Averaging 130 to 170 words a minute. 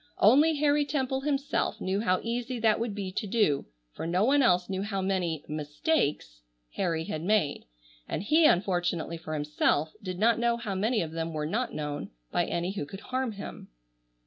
No: average, 190 wpm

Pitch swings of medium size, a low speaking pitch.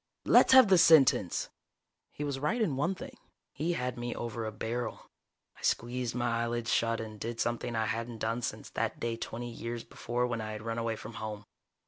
No: narrow, 1.9 semitones; low, 120 Hz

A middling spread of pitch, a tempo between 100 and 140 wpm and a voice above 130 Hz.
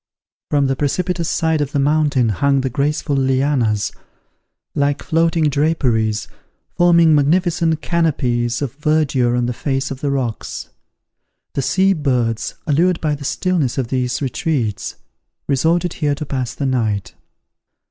Yes: average, 3.8 semitones; slow, 135 wpm; medium, 140 Hz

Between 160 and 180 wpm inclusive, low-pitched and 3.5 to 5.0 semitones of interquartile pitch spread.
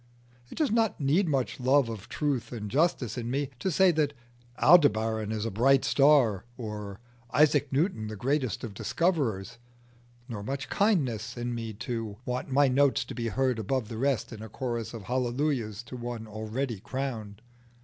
Yes: average, 170 wpm; low, 125 Hz; average, 4.1 semitones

